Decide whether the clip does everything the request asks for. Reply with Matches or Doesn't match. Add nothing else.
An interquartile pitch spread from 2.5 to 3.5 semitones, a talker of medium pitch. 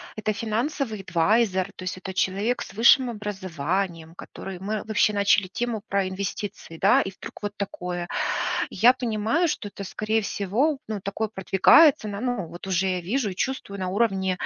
Doesn't match